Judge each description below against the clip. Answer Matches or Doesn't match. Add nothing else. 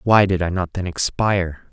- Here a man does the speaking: Matches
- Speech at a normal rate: Doesn't match